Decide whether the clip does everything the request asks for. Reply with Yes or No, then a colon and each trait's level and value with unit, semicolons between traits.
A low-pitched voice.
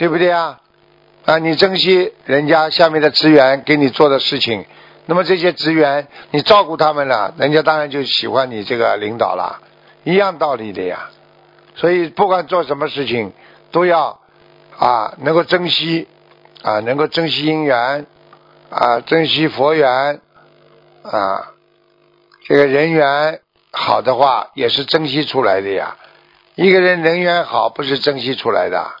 No: medium, 155 Hz